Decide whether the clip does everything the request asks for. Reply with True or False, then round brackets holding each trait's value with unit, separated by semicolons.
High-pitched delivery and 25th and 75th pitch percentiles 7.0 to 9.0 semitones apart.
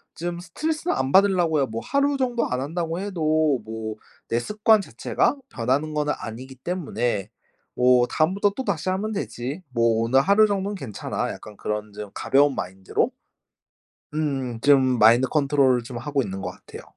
False (140 Hz; 7.6 semitones)